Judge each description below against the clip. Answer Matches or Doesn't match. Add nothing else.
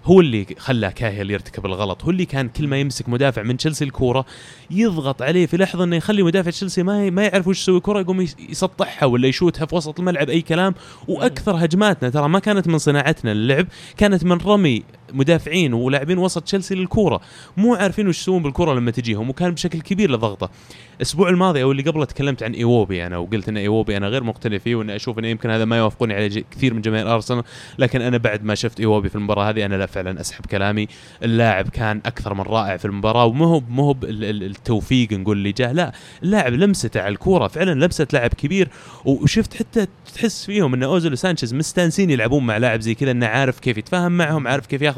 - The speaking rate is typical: Doesn't match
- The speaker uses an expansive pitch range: Matches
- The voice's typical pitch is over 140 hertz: Doesn't match